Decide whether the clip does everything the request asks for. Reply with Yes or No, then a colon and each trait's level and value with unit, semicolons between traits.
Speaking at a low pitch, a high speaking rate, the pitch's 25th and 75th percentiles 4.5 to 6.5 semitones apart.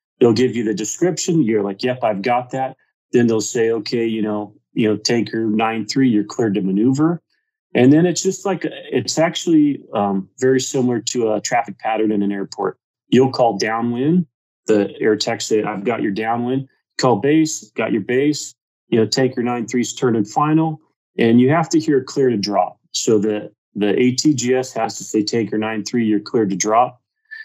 No: low, 120 Hz; average, 195 wpm; average, 5.1 semitones